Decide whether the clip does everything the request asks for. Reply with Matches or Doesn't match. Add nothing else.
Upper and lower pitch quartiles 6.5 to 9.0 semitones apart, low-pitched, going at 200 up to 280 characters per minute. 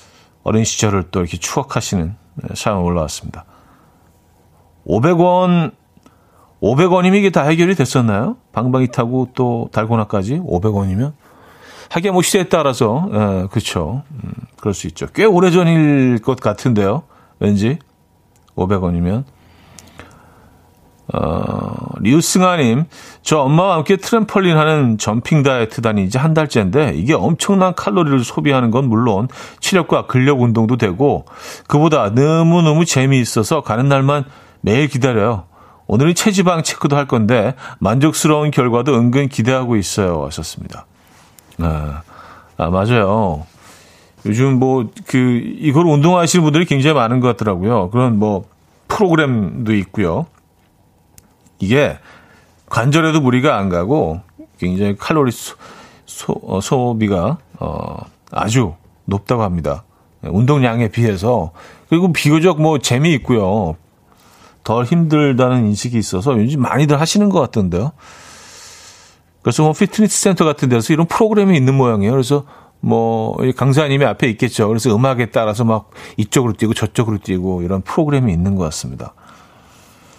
Doesn't match